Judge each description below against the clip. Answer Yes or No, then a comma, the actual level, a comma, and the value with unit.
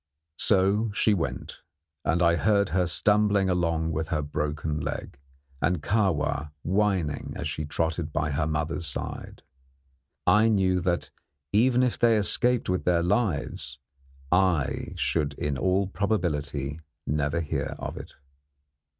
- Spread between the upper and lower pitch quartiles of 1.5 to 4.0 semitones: No, average, 5.0 semitones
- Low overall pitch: Yes, very low, 85 Hz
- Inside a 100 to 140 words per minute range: Yes, slow, 135 wpm